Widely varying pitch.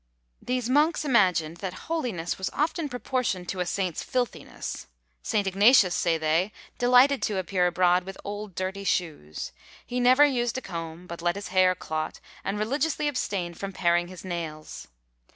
Yes: wide, 6.1 semitones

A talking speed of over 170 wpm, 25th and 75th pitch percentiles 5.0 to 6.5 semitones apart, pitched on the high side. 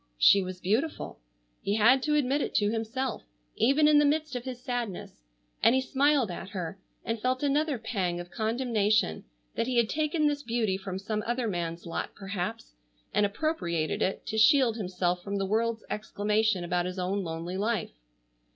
Yes: average, 180 wpm; wide, 5.4 semitones; high, 220 Hz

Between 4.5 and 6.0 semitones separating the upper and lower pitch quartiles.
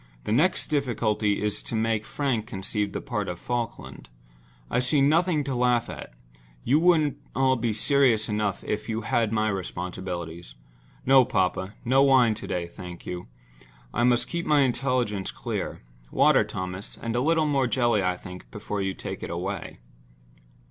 Yes: wide, 5.5 semitones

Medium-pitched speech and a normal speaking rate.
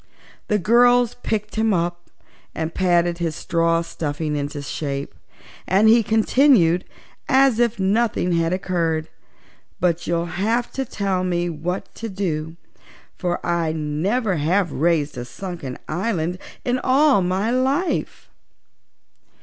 No: medium, 180 Hz; slow, 125 wpm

